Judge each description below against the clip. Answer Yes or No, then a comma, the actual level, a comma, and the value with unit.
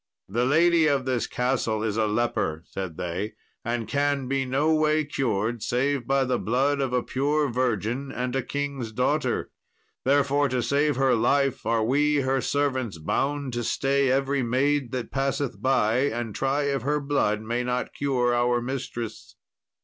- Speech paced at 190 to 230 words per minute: No, average, 165 wpm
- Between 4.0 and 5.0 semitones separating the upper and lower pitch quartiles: No, average, 3.0 semitones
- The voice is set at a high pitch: No, low, 130 Hz